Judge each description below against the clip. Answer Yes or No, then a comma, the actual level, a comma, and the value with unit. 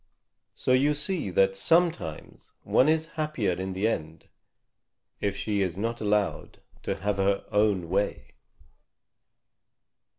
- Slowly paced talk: Yes, slow, 125 wpm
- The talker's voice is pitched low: Yes, low, 105 Hz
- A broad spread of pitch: Yes, wide, 6.4 semitones